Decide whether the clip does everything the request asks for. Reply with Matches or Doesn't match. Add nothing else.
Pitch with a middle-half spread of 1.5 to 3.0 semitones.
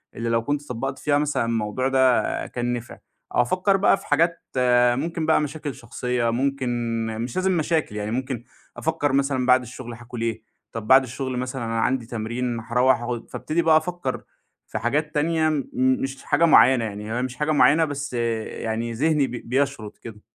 Doesn't match